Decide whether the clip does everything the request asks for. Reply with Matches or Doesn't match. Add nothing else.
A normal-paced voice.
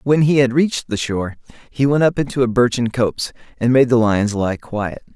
Doesn't match